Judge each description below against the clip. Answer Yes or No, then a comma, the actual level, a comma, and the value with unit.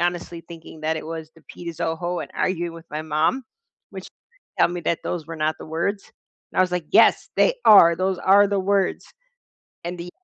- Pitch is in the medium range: Yes, medium, 170 Hz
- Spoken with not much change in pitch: Yes, narrow, 2.3 semitones